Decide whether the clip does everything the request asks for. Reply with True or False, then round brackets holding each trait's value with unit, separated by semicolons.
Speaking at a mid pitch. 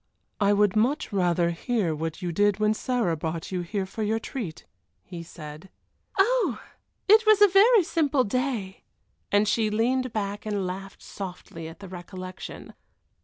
False (205 Hz)